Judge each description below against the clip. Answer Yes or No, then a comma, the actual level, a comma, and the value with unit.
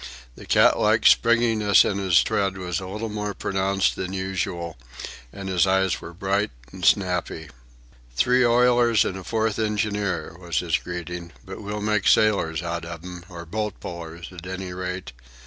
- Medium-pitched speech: No, very low, 95 Hz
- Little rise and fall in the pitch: No, average, 3.0 semitones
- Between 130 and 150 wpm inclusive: No, average, 165 wpm